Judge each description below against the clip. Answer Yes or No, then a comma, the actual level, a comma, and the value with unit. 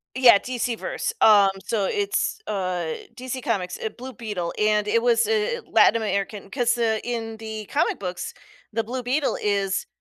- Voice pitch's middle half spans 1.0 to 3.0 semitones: No, average, 3.6 semitones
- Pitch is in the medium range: No, high, 225 Hz